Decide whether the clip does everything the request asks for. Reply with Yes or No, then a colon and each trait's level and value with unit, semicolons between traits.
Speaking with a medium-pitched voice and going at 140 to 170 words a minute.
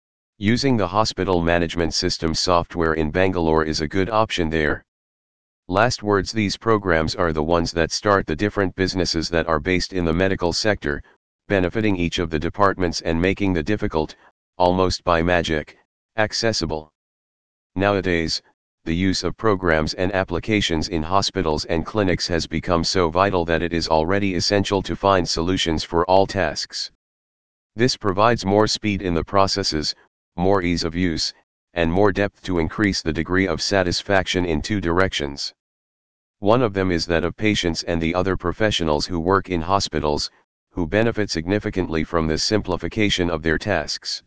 No: very low, 90 Hz; average, 160 wpm